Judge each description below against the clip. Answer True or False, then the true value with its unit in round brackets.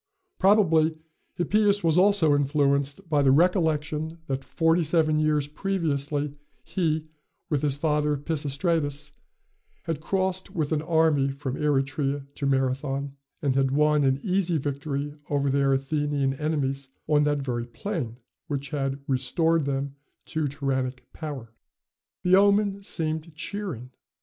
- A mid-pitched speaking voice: True (150 Hz)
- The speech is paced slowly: True (130 wpm)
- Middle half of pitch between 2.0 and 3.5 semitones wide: True (2.9 semitones)